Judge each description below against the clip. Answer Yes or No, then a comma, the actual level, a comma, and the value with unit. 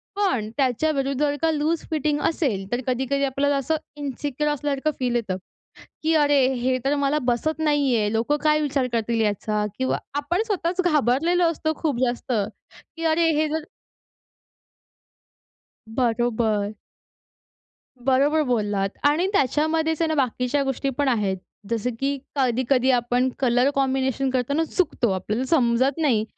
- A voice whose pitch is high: Yes, very high, 270 Hz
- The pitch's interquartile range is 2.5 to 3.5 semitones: No, average, 3.9 semitones